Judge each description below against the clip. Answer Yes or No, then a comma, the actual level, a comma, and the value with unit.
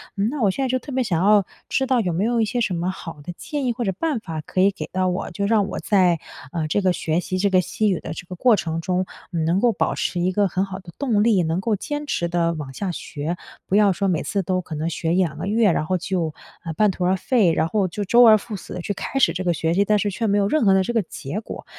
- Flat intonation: No, average, 3.8 semitones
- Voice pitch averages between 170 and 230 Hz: Yes, high, 190 Hz